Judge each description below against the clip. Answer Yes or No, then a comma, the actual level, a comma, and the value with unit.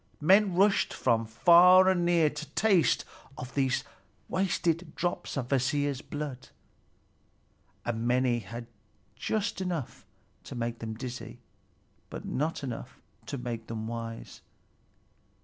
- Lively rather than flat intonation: Yes, wide, 6.6 semitones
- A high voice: No, medium, 140 Hz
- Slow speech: Yes, slow, 120 wpm